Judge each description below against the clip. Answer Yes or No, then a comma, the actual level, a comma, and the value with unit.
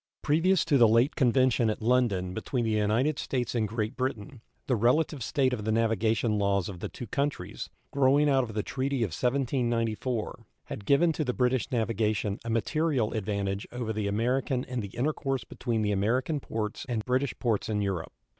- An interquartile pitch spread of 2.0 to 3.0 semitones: No, average, 3.6 semitones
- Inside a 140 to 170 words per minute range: No, average, 185 wpm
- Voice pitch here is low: Yes, low, 120 Hz